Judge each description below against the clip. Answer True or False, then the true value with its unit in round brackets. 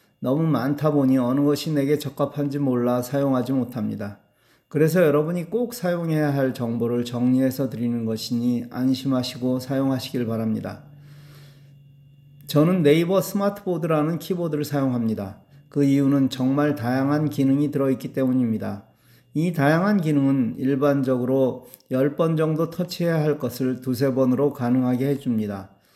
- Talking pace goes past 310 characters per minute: True (330 characters per minute)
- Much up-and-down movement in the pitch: False (2.6 semitones)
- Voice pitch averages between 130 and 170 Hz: True (140 Hz)